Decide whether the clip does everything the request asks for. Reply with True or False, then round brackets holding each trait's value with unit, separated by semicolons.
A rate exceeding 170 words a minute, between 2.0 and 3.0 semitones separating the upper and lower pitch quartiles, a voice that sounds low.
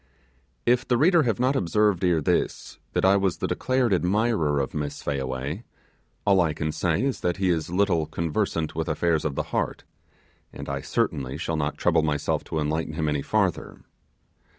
False (180 wpm; 5.0 semitones; 85 Hz)